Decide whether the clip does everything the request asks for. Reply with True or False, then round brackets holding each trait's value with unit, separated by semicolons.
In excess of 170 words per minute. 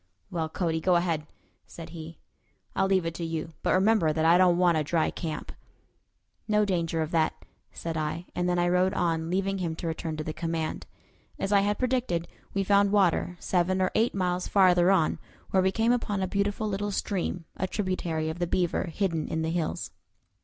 True (200 wpm)